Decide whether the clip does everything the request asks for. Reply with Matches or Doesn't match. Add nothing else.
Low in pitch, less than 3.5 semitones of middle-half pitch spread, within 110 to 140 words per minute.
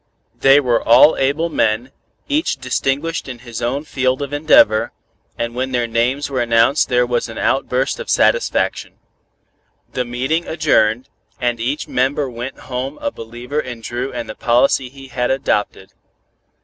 Doesn't match